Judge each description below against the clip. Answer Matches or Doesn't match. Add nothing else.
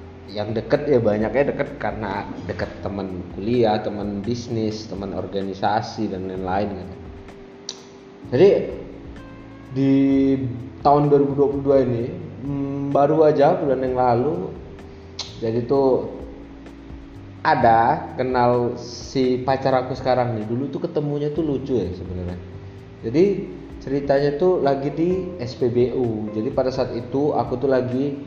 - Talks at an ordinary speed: Matches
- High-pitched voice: Doesn't match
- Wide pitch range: Matches